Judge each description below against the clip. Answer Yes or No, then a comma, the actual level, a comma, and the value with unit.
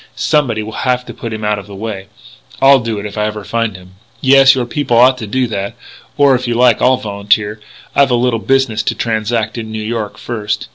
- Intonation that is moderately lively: Yes, average, 3.1 semitones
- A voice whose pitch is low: Yes, low, 115 Hz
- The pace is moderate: No, fast, 230 wpm